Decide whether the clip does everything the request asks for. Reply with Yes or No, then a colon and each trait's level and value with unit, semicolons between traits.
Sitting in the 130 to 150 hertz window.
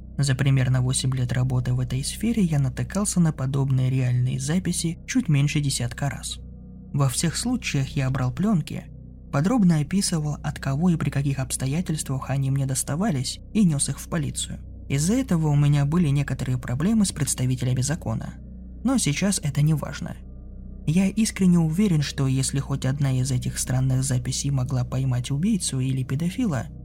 Yes: medium, 140 Hz